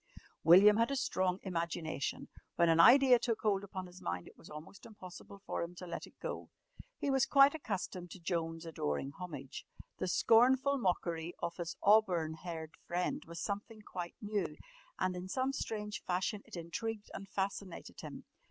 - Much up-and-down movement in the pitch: No, average, 4.0 semitones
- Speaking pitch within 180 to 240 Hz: Yes, medium, 185 Hz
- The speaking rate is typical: Yes, average, 170 wpm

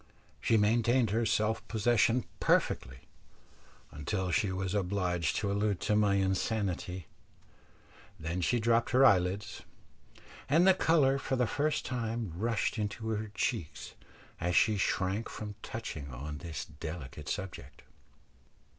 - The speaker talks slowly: Yes, slow, 130 wpm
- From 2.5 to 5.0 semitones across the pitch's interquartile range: Yes, average, 4.3 semitones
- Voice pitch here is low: Yes, low, 105 Hz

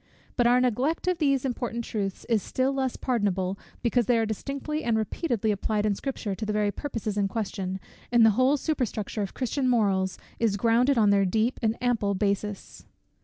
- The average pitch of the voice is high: Yes, high, 225 Hz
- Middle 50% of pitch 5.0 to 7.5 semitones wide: No, average, 3.7 semitones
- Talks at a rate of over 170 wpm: Yes, average, 185 wpm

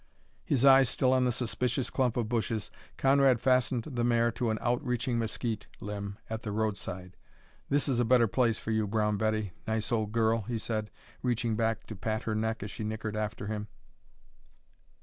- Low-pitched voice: Yes, low, 115 Hz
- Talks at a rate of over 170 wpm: Yes, average, 185 wpm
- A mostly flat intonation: Yes, narrow, 2.2 semitones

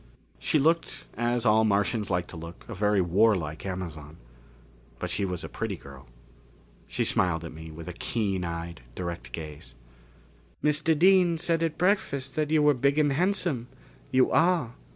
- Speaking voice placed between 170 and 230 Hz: No, low, 110 Hz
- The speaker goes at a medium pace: Yes, average, 165 wpm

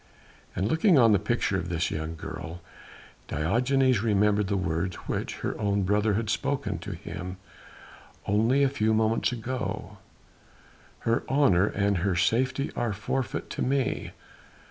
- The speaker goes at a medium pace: Yes, average, 145 wpm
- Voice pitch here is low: Yes, low, 105 Hz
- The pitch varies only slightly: No, average, 4.7 semitones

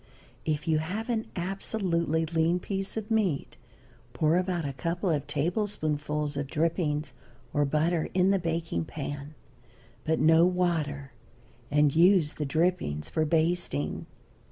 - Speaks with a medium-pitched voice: Yes, medium, 160 Hz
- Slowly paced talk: Yes, slow, 130 wpm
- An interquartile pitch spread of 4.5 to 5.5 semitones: No, average, 3.3 semitones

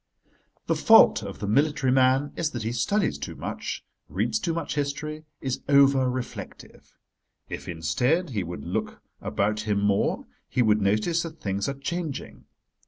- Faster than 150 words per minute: Yes, average, 160 wpm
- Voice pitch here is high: No, low, 130 Hz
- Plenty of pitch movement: Yes, wide, 6.2 semitones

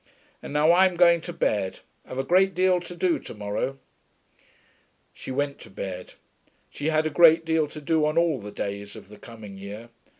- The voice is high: No, medium, 150 Hz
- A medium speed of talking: Yes, average, 195 wpm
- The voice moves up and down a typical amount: No, wide, 8.2 semitones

